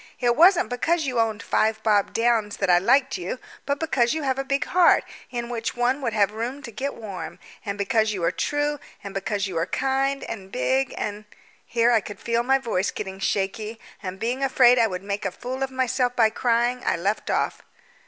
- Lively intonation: No, average, 4.2 semitones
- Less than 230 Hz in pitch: No, high, 235 Hz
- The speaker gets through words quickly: Yes, fast, 215 wpm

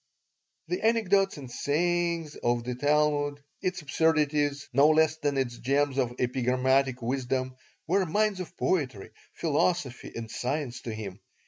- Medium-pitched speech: Yes, medium, 145 Hz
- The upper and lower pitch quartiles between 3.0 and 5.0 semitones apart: Yes, average, 4.2 semitones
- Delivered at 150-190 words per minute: No, slow, 135 wpm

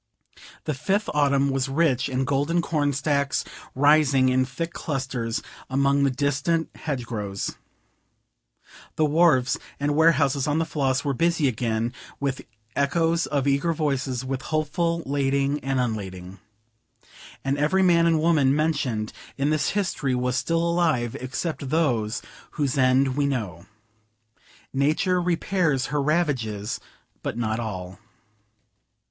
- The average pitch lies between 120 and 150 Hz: Yes, medium, 140 Hz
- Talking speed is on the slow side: Yes, slow, 125 wpm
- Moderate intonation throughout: Yes, average, 3.4 semitones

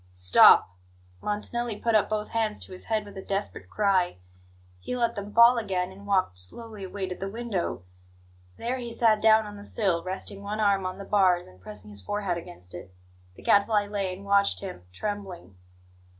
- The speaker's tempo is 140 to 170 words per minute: No, average, 190 wpm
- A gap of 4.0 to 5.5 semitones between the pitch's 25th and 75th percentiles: No, average, 2.8 semitones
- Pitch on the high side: Yes, high, 200 Hz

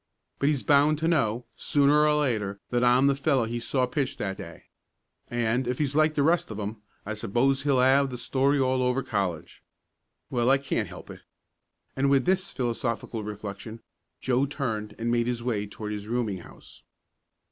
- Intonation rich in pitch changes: No, average, 3.9 semitones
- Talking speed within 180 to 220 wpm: Yes, average, 185 wpm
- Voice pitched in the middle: No, low, 125 Hz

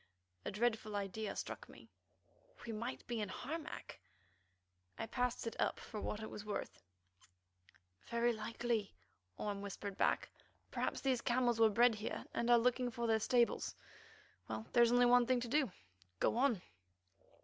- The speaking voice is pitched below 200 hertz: No, high, 230 Hz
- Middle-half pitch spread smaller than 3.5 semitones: Yes, narrow, 2.5 semitones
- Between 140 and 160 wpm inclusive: Yes, average, 155 wpm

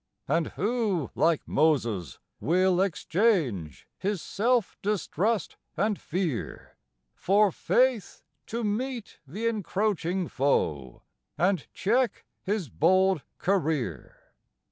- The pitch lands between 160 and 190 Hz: Yes, medium, 185 Hz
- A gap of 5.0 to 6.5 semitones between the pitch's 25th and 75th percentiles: Yes, average, 5.3 semitones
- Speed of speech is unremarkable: No, slow, 95 wpm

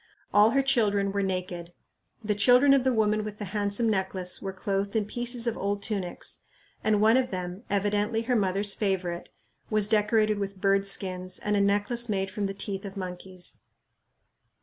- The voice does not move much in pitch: Yes, narrow, 2.0 semitones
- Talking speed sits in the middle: Yes, average, 175 wpm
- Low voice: No, high, 205 Hz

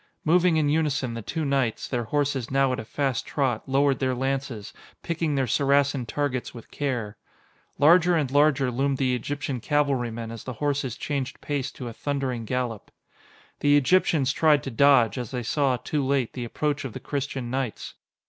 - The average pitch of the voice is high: No, low, 135 Hz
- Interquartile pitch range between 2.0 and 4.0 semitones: Yes, average, 2.7 semitones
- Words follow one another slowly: No, average, 175 wpm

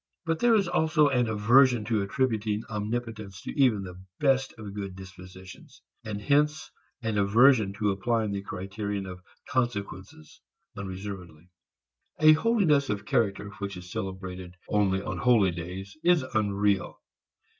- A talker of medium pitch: No, low, 105 Hz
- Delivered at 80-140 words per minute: Yes, slow, 135 wpm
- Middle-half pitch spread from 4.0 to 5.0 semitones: Yes, average, 4.3 semitones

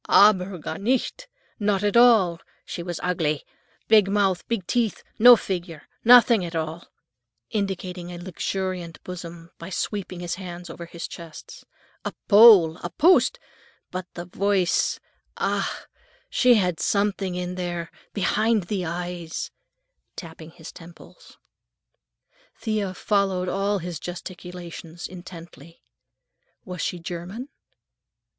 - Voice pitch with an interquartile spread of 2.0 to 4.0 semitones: Yes, average, 3.0 semitones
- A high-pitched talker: No, medium, 180 Hz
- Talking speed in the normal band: No, slow, 120 wpm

